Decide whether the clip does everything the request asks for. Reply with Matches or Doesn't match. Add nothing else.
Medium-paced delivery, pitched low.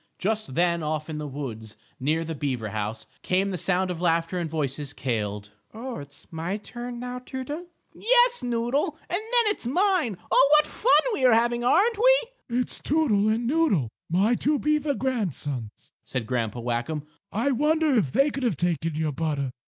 Doesn't match